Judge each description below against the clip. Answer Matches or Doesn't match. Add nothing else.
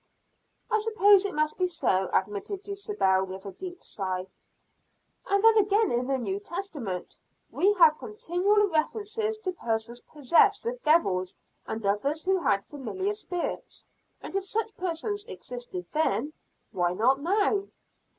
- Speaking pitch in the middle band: Doesn't match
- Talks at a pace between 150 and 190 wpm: Doesn't match